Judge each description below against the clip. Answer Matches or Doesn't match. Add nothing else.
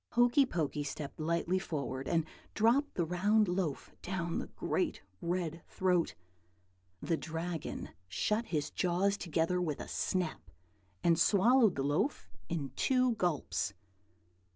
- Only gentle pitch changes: Doesn't match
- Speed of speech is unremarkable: Doesn't match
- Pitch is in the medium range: Matches